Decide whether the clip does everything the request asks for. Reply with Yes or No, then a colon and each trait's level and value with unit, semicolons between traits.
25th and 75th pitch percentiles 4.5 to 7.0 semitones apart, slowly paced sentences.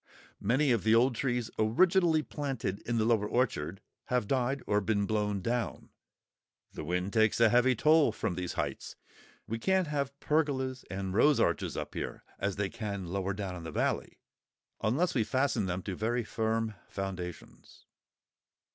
No: average, 4.9 semitones; average, 165 wpm